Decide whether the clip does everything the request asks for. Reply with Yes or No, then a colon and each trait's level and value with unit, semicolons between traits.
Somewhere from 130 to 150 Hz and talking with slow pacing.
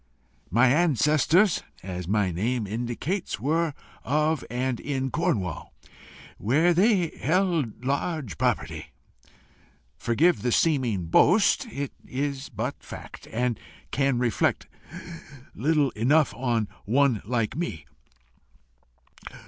Yes: low, 135 Hz; slow, 100 wpm